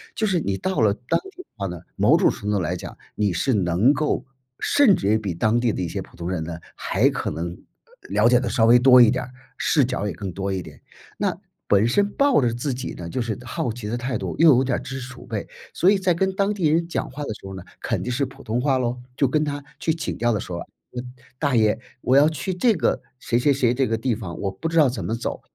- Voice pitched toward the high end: No, low, 120 Hz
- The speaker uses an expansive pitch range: Yes, wide, 5.7 semitones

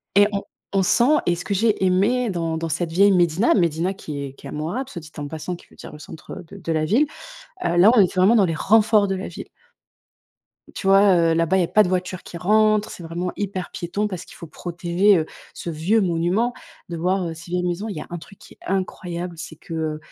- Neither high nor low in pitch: Yes, medium, 180 Hz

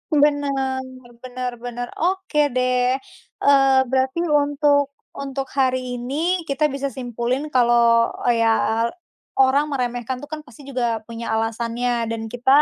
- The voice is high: Yes, very high, 260 Hz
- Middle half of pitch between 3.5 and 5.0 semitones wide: No, average, 2.8 semitones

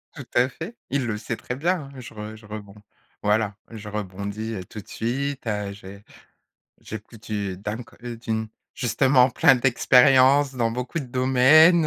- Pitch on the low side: Yes, low, 115 Hz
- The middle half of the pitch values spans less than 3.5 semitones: No, average, 3.8 semitones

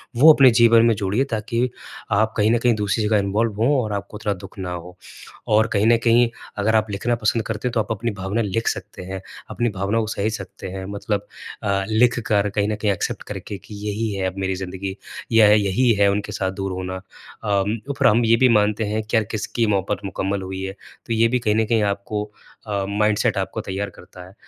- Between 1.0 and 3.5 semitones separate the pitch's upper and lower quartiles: Yes, narrow, 2.5 semitones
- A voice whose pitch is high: No, low, 105 Hz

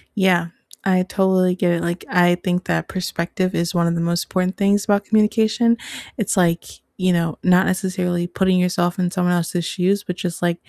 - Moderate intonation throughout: No, narrow, 1.6 semitones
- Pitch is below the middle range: No, medium, 180 Hz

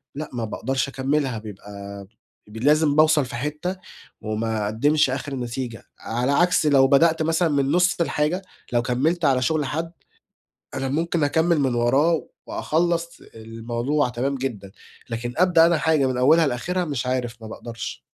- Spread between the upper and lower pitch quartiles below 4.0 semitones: No, average, 4.9 semitones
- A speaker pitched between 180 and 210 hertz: No, low, 135 Hz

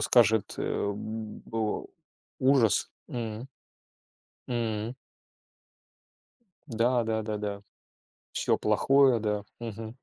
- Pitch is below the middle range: Yes, low, 110 Hz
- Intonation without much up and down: Yes, narrow, 2.1 semitones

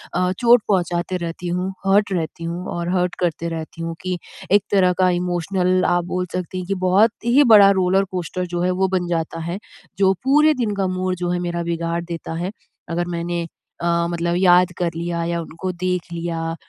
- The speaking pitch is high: No, medium, 180 Hz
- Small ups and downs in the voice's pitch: Yes, narrow, 1.6 semitones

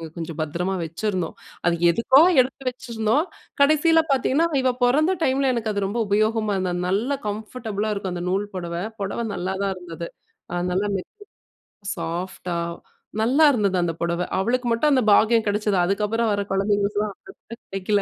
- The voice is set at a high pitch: Yes, high, 205 Hz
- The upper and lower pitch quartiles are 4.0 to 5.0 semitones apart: Yes, average, 4.3 semitones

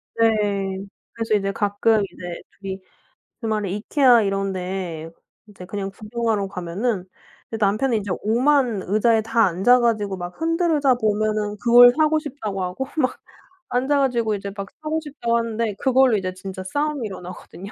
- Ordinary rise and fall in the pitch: Yes, average, 3.8 semitones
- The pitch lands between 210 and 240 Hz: Yes, high, 215 Hz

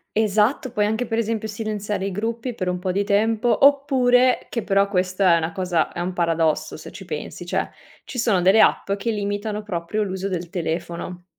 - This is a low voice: No, high, 205 Hz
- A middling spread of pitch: Yes, average, 3.5 semitones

